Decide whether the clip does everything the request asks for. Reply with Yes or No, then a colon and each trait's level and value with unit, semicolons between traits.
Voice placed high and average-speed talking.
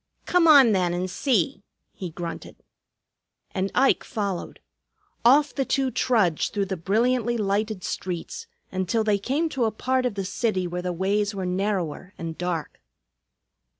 Yes: high, 200 Hz; average, 150 wpm